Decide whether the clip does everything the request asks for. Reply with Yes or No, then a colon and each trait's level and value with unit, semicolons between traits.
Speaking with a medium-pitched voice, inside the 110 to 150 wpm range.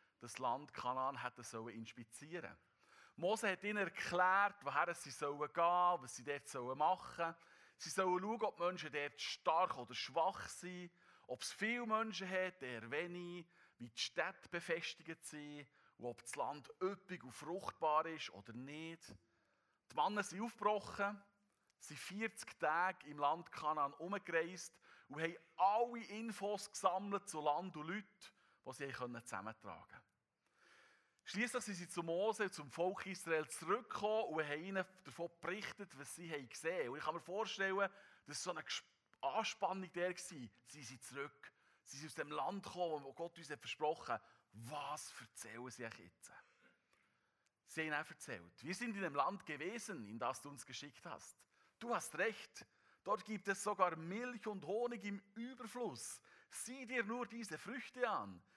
No: medium, 170 Hz; average, 160 wpm